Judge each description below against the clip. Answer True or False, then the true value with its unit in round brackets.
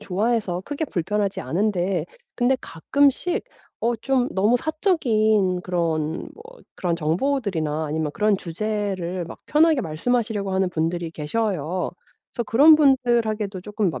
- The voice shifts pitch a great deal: True (5.7 semitones)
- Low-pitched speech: False (205 Hz)